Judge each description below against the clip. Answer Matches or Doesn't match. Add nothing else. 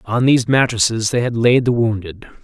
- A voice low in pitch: Matches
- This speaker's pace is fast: Doesn't match